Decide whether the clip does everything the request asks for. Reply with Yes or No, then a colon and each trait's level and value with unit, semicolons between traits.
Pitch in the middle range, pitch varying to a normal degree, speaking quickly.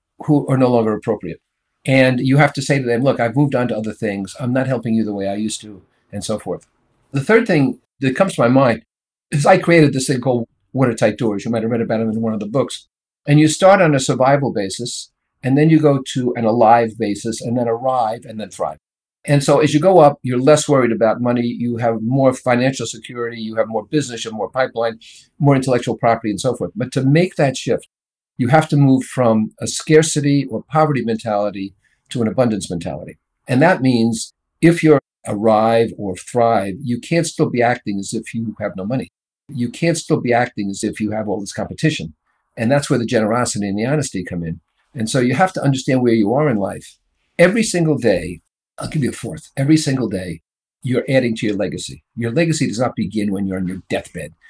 No: low, 120 Hz; average, 4.3 semitones; fast, 225 wpm